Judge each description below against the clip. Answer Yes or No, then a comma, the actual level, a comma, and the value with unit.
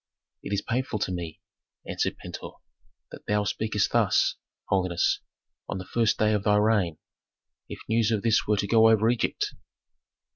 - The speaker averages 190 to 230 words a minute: No, average, 160 wpm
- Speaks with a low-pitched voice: Yes, low, 105 Hz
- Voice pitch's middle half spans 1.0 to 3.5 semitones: Yes, narrow, 2.4 semitones